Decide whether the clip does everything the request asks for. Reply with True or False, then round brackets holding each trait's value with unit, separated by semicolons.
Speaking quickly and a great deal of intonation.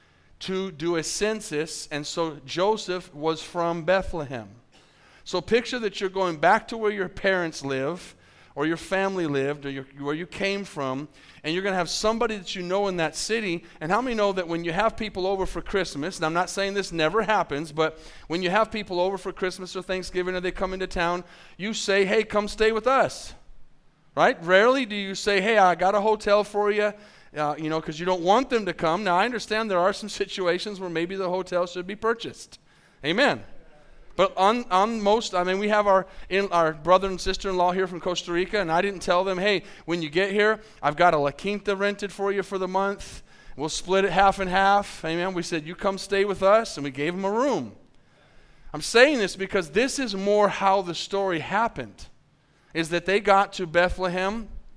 False (215 wpm; 3.0 semitones)